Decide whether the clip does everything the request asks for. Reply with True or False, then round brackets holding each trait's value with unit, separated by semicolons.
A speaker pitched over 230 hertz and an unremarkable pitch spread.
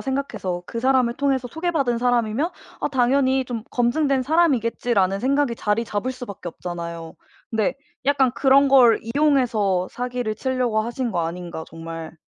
True (245 Hz; 4.5 semitones)